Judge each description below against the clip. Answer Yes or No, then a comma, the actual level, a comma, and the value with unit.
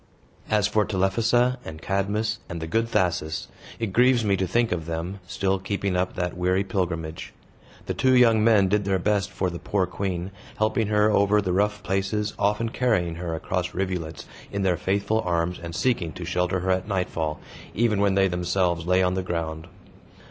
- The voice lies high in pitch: No, very low, 95 Hz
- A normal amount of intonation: Yes, average, 3.0 semitones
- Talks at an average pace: Yes, average, 185 wpm